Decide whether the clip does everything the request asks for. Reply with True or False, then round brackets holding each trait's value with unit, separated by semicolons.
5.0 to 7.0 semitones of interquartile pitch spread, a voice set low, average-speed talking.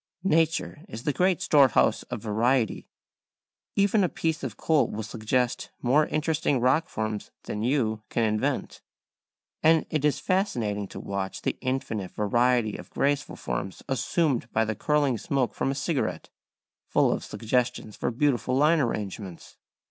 True (5.5 semitones; 125 Hz; 150 wpm)